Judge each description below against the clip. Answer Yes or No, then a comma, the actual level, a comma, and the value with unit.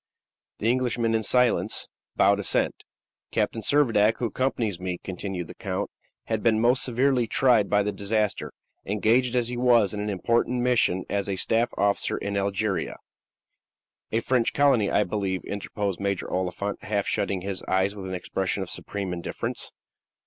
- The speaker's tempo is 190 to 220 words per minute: No, average, 165 wpm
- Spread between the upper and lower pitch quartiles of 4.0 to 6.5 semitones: No, average, 3.2 semitones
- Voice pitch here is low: Yes, low, 105 Hz